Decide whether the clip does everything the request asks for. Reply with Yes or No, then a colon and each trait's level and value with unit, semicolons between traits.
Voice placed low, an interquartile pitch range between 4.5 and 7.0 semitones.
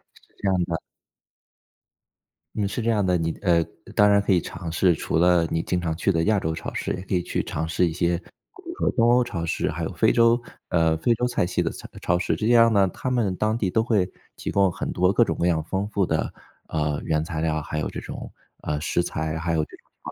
No: very low, 90 Hz; average, 4.0 semitones